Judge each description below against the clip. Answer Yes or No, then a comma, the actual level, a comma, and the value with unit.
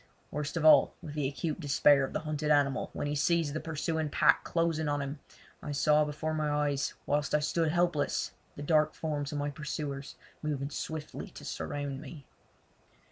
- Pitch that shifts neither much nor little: No, narrow, 1.5 semitones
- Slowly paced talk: No, average, 185 wpm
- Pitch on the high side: No, medium, 150 Hz